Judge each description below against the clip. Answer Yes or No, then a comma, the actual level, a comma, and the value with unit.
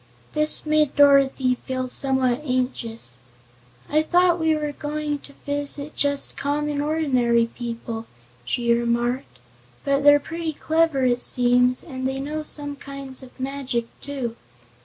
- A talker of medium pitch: No, very high, 275 Hz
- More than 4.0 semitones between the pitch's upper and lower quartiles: No, average, 3.0 semitones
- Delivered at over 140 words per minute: No, slow, 135 wpm